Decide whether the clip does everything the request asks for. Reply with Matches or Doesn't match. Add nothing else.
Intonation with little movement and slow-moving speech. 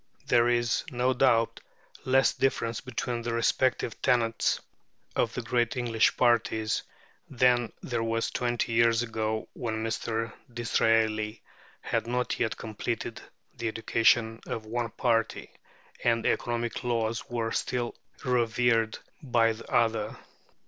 Matches